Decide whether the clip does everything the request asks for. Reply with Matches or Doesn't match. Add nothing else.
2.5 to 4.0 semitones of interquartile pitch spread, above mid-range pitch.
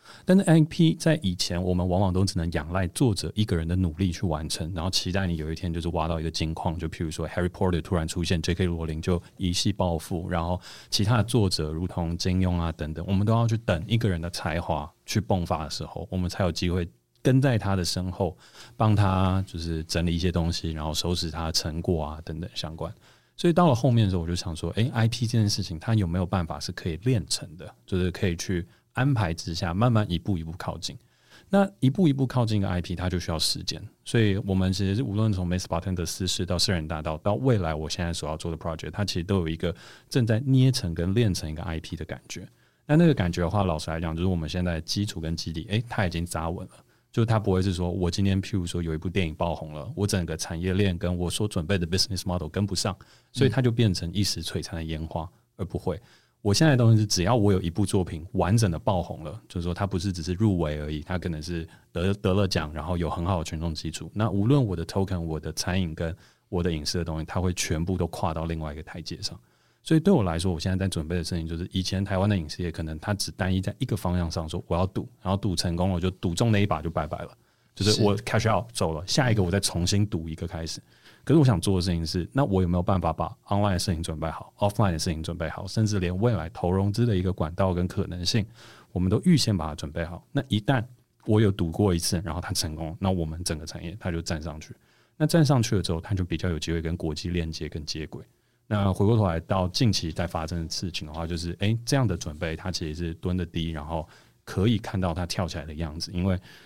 Doesn't match